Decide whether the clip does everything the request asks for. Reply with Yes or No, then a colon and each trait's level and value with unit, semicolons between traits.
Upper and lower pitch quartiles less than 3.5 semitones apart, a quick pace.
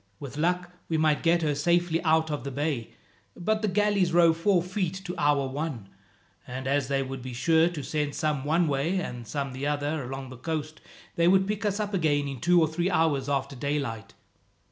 No: average, 3.9 semitones; fast, 210 wpm